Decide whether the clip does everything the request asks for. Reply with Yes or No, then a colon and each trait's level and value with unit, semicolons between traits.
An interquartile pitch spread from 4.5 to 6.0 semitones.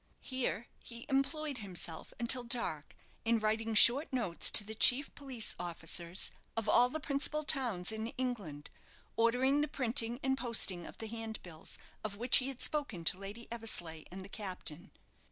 Yes: average, 4.9 semitones